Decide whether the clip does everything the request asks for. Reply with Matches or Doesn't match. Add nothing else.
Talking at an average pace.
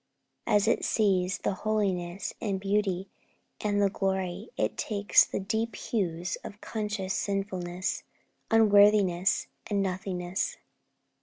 Doesn't match